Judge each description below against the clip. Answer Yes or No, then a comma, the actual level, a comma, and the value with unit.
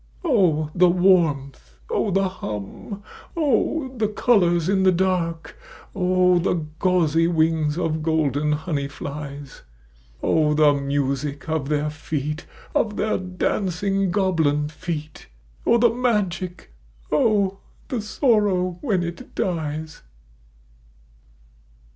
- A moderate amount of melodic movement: Yes, average, 4.2 semitones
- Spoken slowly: Yes, slow, 110 wpm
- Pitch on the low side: No, medium, 170 Hz